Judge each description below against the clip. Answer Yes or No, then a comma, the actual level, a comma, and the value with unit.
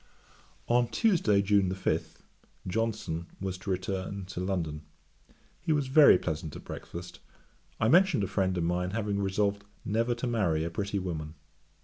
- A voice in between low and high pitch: No, low, 100 Hz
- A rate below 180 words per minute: Yes, average, 150 wpm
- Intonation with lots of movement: No, average, 3.9 semitones